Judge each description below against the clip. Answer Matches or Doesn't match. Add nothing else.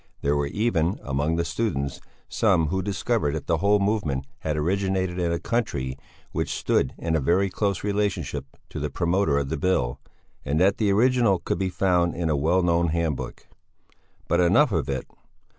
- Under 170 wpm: Doesn't match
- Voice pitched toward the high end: Doesn't match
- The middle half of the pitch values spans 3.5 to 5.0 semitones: Matches